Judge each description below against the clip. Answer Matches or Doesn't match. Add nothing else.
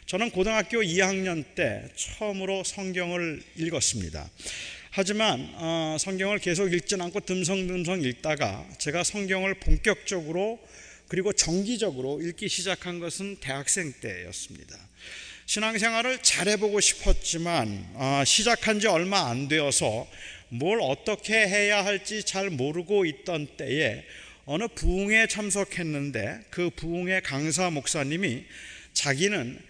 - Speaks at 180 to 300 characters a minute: Matches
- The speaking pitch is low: Doesn't match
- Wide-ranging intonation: Doesn't match